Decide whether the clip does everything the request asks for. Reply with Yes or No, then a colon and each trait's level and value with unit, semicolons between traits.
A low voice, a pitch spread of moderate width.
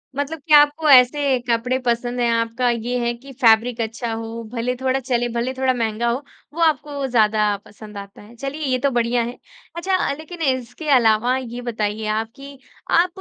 No: high, 245 Hz; average, 3.1 semitones